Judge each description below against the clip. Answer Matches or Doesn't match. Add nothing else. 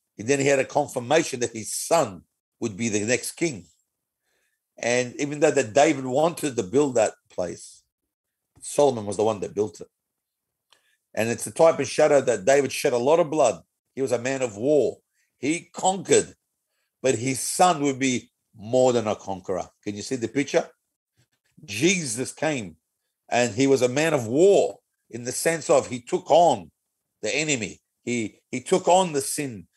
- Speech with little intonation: Doesn't match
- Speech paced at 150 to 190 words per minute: Matches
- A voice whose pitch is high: Doesn't match